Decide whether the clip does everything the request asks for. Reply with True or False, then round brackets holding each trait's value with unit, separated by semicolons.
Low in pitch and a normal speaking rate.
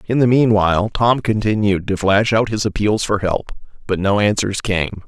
True (105 Hz; 190 wpm)